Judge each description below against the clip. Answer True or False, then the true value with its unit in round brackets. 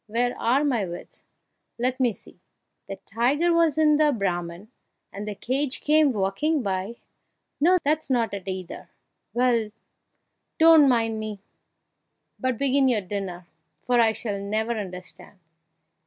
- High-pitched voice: True (235 Hz)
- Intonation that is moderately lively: False (5.7 semitones)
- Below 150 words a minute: True (140 wpm)